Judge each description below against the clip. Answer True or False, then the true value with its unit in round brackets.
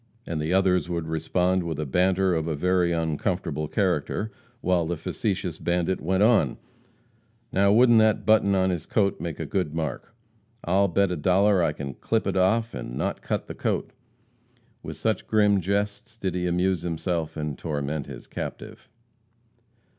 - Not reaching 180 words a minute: True (170 wpm)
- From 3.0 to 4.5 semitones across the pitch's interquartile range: True (3.5 semitones)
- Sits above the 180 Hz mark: False (90 Hz)